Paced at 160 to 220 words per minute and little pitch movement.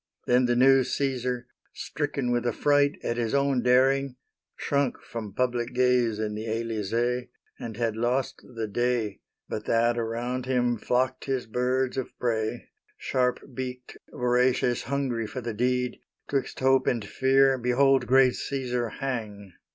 No: average, 145 wpm; narrow, 1.9 semitones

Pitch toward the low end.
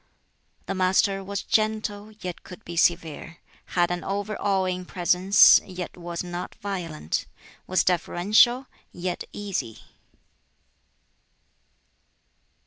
No: medium, 185 Hz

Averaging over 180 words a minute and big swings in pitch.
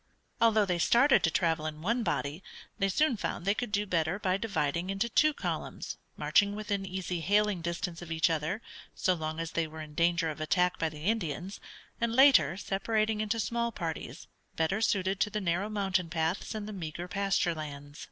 No: average, 190 wpm; average, 4.4 semitones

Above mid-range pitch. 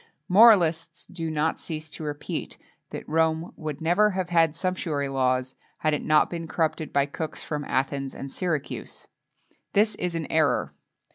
No: medium, 160 Hz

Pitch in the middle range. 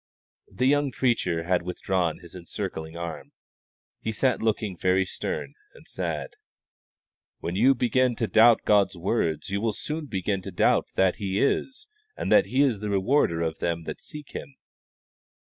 No: low, 100 Hz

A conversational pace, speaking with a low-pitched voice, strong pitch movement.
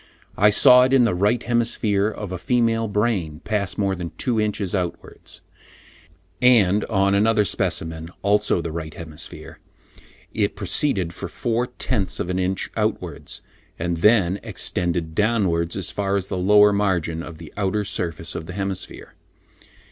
No: average, 155 wpm; low, 100 Hz; average, 3.6 semitones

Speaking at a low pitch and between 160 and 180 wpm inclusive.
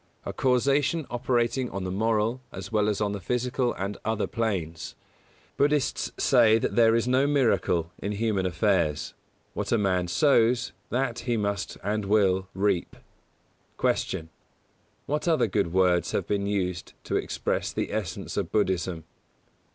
No: low, 110 Hz; average, 150 wpm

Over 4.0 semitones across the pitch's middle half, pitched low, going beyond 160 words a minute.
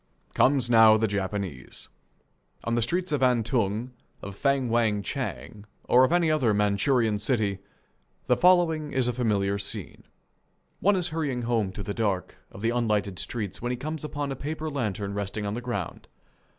Yes: average, 5.2 semitones; low, 115 Hz; average, 170 wpm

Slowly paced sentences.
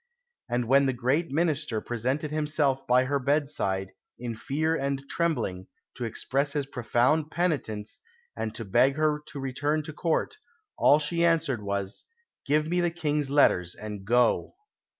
No: average, 150 wpm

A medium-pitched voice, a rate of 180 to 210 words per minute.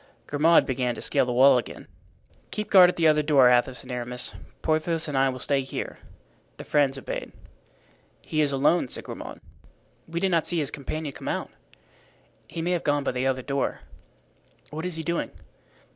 Yes: medium, 145 Hz; average, 190 wpm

